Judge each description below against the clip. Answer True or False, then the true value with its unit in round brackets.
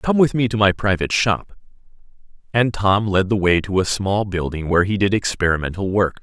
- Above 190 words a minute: True (200 wpm)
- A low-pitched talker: True (100 Hz)